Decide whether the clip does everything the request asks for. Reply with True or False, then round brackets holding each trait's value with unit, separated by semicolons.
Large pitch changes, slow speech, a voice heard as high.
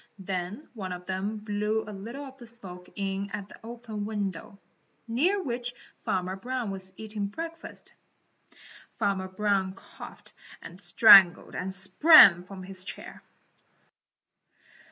False (3.3 semitones; 130 wpm; 200 Hz)